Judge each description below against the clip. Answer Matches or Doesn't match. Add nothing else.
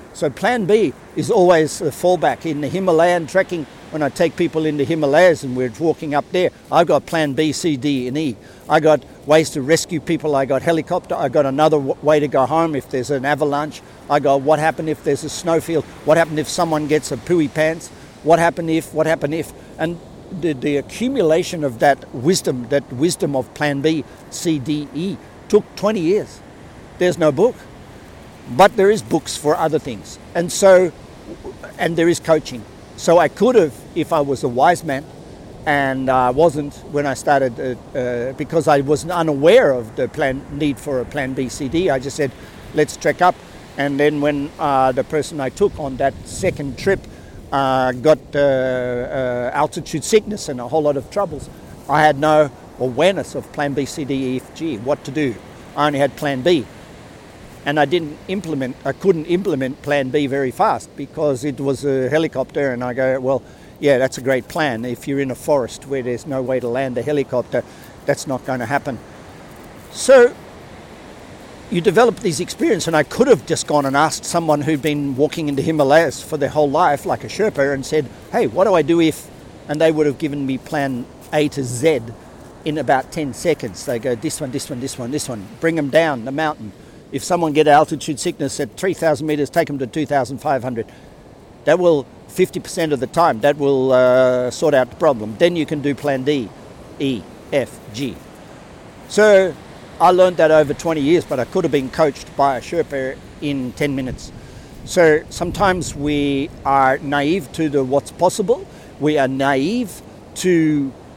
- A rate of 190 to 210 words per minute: Matches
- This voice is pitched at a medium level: Matches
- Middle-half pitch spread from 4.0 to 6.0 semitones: Doesn't match